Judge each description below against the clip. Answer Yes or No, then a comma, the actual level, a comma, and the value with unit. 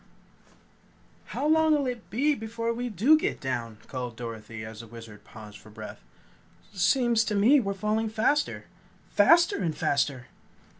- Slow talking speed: No, average, 145 wpm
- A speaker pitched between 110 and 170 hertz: No, high, 210 Hz